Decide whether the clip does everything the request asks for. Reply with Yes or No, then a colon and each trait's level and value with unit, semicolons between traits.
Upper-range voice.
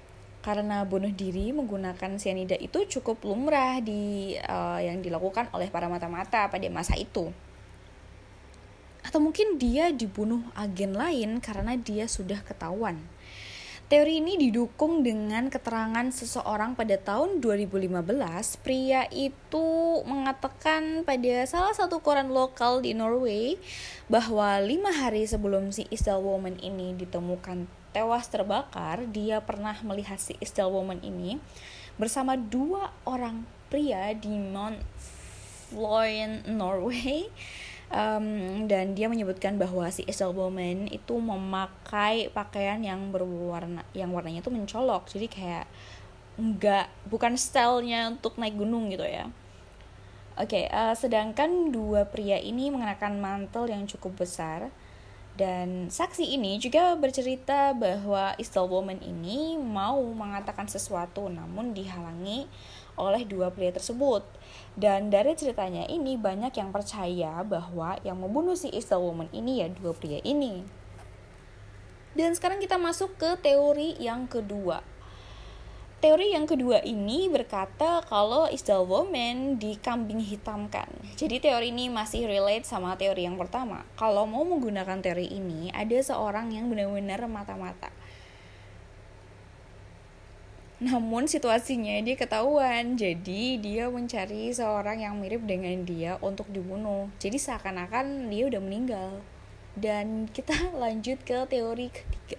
Yes: high, 210 Hz